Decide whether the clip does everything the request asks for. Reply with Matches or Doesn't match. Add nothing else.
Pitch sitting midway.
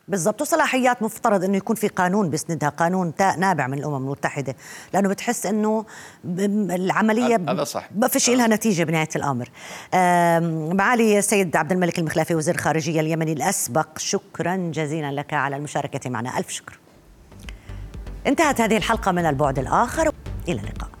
Matches